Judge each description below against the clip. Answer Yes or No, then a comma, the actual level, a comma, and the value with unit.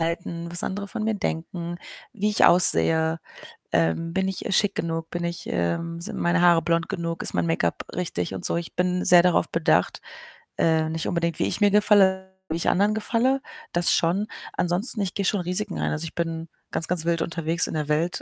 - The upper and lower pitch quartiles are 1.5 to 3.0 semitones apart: Yes, narrow, 2.5 semitones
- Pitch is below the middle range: No, medium, 170 Hz